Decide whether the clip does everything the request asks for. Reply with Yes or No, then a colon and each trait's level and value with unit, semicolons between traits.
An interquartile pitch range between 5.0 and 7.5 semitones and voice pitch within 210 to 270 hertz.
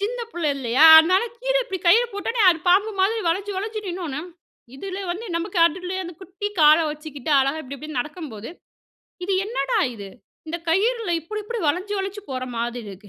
No: wide, 5.5 semitones; very high, 355 Hz